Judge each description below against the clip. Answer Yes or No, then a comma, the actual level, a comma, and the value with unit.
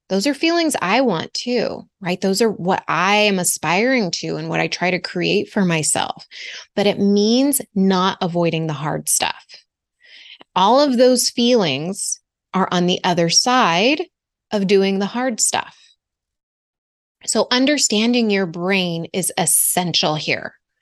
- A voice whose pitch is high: Yes, high, 200 Hz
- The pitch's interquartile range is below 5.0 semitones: No, wide, 5.5 semitones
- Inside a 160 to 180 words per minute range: No, average, 145 wpm